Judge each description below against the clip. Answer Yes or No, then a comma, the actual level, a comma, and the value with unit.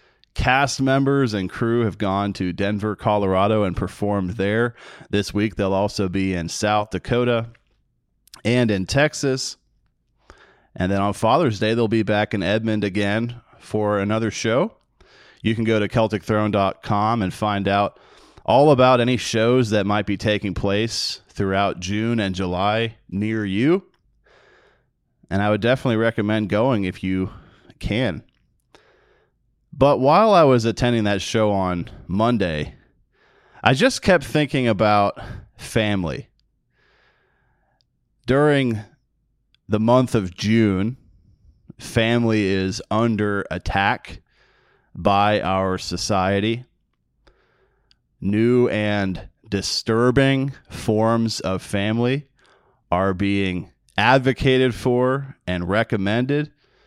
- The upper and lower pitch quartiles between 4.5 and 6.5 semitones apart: No, average, 3.3 semitones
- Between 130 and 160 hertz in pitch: No, low, 105 Hz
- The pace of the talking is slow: Yes, slow, 115 wpm